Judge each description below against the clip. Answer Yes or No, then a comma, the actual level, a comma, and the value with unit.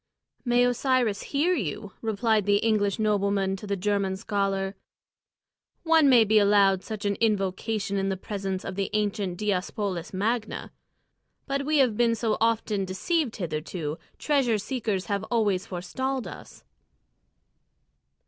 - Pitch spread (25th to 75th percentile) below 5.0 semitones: Yes, average, 3.0 semitones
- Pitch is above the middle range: Yes, high, 205 Hz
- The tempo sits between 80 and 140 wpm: Yes, slow, 135 wpm